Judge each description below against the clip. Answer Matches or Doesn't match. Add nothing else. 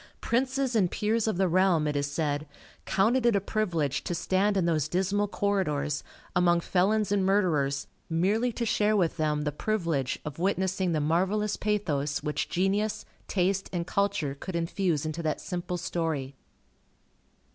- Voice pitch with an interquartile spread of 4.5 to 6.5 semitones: Matches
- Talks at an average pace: Matches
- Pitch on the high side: Doesn't match